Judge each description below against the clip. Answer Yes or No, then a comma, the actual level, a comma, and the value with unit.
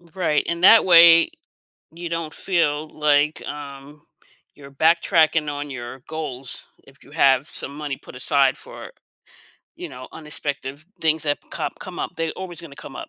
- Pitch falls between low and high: Yes, medium, 150 Hz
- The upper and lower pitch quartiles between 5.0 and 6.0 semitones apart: No, average, 2.9 semitones